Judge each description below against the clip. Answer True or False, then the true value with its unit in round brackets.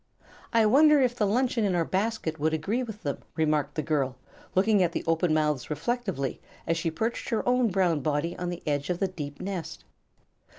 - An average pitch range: False (6.1 semitones)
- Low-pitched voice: False (175 Hz)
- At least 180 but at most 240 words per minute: True (200 wpm)